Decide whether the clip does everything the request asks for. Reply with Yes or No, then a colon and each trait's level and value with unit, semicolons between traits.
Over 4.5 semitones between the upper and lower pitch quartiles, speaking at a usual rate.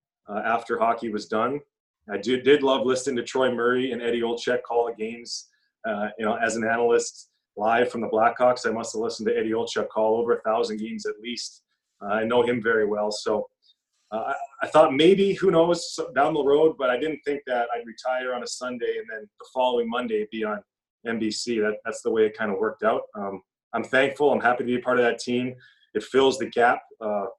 No: average, 5.1 semitones; fast, 225 wpm